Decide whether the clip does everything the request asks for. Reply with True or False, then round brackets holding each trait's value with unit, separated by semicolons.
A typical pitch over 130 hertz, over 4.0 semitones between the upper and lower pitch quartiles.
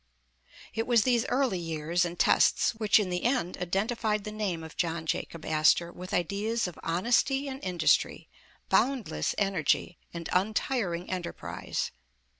True (185 Hz; 4.9 semitones)